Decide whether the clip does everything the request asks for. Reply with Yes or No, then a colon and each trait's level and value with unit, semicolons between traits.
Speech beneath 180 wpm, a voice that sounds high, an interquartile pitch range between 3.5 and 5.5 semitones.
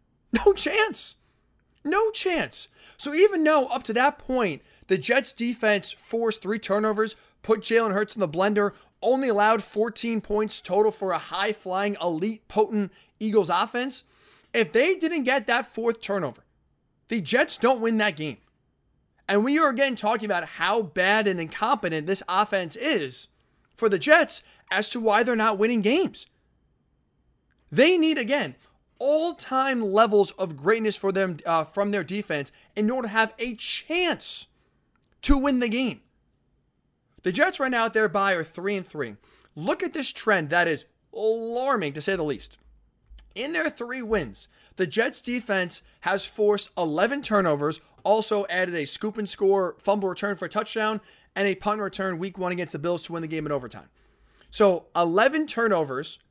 Yes: average, 170 wpm; high, 215 Hz; average, 4.5 semitones